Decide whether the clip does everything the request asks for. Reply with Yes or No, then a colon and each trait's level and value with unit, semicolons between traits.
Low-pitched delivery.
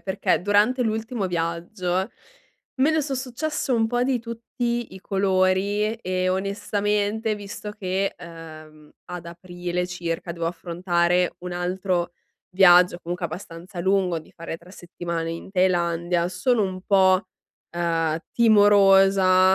No: medium, 185 Hz